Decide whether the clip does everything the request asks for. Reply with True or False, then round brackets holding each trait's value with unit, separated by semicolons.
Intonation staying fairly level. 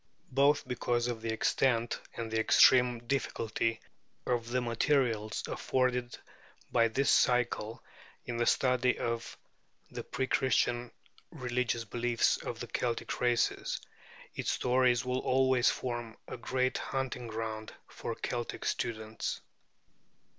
True (1.7 semitones)